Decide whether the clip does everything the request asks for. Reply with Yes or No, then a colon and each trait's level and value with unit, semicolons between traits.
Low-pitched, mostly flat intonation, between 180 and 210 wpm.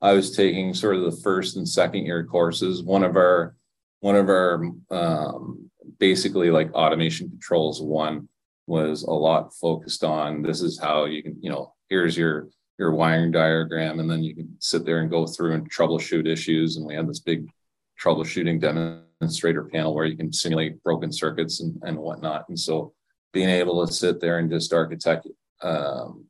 Yes: very low, 80 Hz; narrow, 1.3 semitones; average, 185 wpm